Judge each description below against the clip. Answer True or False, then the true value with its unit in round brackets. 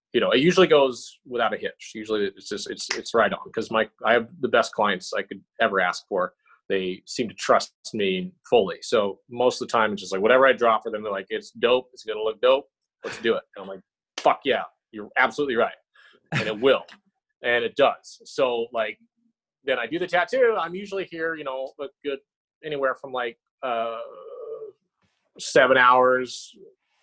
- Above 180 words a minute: True (205 wpm)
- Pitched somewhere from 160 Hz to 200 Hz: True (190 Hz)